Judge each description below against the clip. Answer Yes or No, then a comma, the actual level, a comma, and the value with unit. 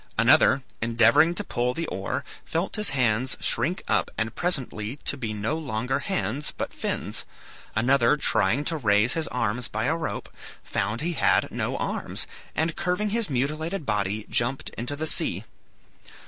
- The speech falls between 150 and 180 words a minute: Yes, average, 160 wpm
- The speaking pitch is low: Yes, low, 130 Hz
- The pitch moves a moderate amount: No, wide, 6.1 semitones